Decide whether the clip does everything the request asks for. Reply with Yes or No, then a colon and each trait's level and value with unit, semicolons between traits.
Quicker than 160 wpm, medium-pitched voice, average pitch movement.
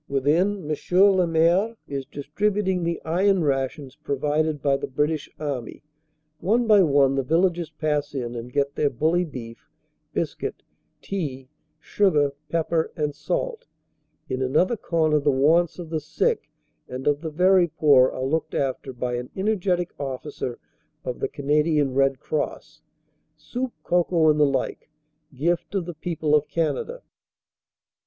No: average, 150 wpm; medium, 150 Hz; average, 4.0 semitones